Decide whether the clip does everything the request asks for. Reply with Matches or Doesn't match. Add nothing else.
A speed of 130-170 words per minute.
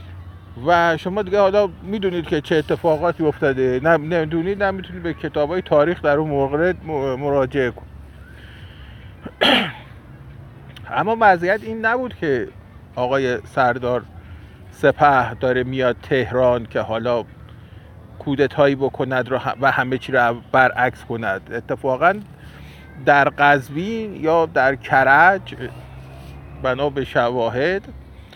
Doesn't match